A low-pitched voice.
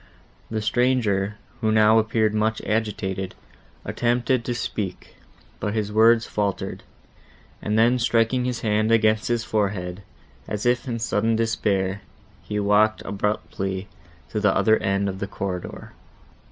Yes: low, 110 Hz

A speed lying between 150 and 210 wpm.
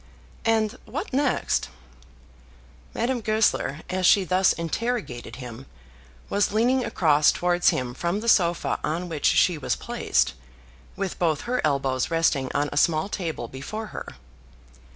No: slow, 135 wpm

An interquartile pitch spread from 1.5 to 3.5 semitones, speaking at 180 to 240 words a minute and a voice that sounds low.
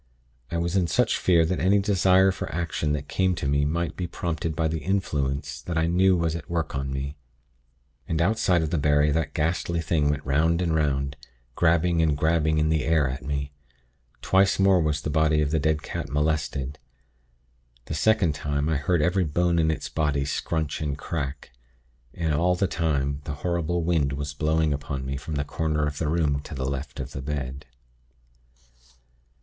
Yes: average, 2.8 semitones; average, 190 wpm; very low, 80 Hz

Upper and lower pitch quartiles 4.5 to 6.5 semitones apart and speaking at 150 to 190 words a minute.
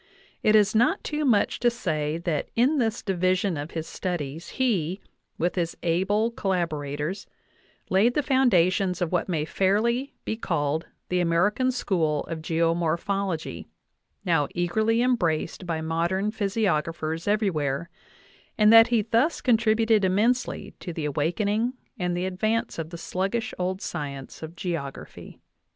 No: average, 4.9 semitones; average, 140 wpm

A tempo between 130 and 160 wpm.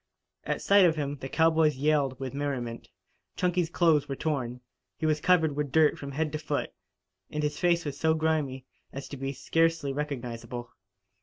No: average, 175 wpm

